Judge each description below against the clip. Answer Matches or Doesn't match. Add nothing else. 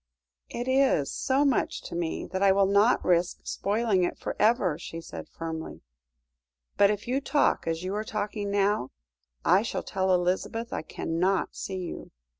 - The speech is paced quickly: Doesn't match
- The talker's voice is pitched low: Doesn't match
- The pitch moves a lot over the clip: Doesn't match